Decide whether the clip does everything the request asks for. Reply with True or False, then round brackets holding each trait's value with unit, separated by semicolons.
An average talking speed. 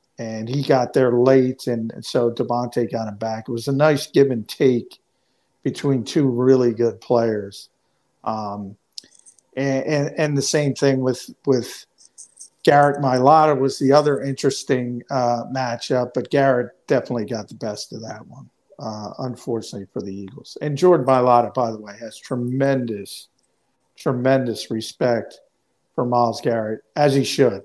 True (155 wpm)